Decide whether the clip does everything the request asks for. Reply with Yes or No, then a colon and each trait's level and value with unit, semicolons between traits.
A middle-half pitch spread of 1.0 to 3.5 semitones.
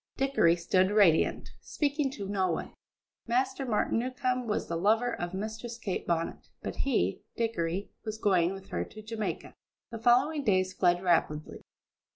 No: average, 5.1 semitones